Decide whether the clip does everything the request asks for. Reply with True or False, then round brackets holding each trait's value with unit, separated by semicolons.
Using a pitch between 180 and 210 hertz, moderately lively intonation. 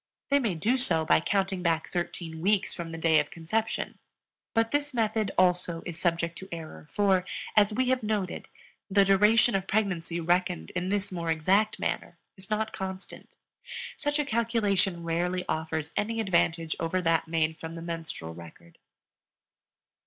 True (185 Hz; 4.2 semitones)